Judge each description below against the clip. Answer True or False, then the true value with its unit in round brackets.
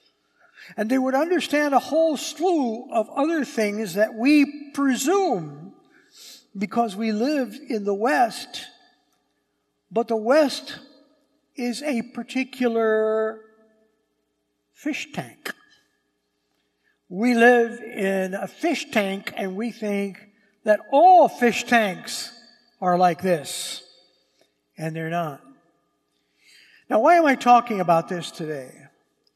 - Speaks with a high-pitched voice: True (235 Hz)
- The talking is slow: True (110 wpm)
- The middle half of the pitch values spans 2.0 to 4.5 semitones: False (5.0 semitones)